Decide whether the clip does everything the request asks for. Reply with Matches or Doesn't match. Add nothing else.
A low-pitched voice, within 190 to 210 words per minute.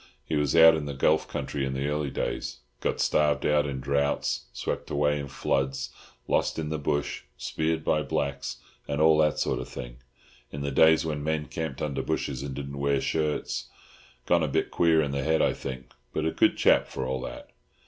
Matches